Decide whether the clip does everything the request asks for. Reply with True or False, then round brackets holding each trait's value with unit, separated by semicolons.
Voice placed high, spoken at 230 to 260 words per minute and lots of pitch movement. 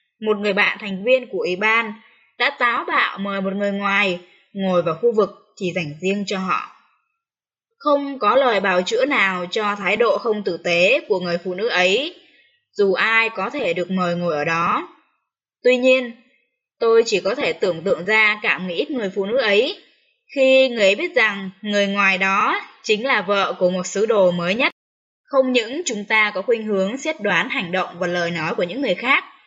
False (210 Hz; 205 wpm; 5.7 semitones)